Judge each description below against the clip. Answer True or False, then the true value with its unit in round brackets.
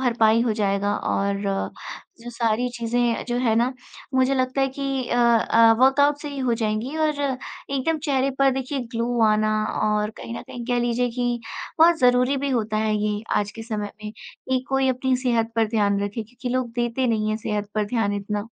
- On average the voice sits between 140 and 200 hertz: False (240 Hz)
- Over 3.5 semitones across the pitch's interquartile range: False (3.2 semitones)